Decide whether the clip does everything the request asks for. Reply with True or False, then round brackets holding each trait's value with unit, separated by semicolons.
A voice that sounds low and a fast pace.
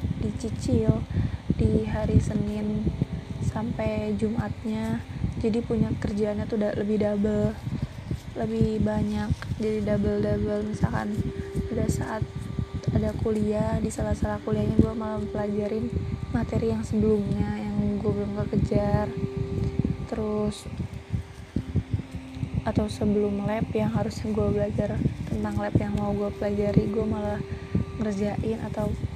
False (110 Hz; 115 wpm)